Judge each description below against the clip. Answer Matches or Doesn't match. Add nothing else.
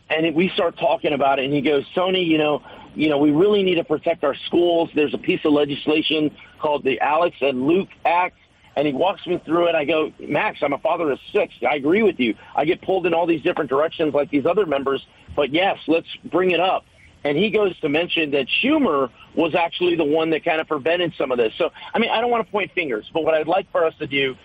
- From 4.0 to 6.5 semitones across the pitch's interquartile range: Doesn't match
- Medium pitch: Matches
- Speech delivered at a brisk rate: Matches